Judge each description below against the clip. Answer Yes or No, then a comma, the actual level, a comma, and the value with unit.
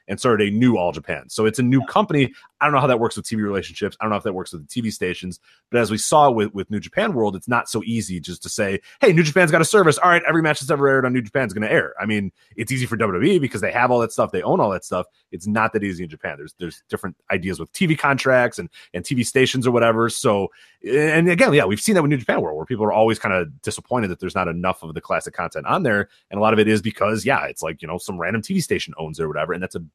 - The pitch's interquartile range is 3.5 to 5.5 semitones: Yes, average, 5.2 semitones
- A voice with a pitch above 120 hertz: No, low, 115 Hz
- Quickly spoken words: Yes, fast, 305 wpm